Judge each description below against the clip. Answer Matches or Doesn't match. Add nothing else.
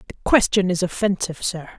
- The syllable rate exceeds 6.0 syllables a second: Matches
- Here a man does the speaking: Doesn't match